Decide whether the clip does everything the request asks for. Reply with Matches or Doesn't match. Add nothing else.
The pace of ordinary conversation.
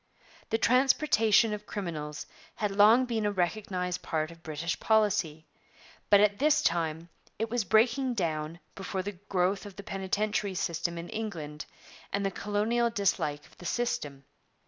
Matches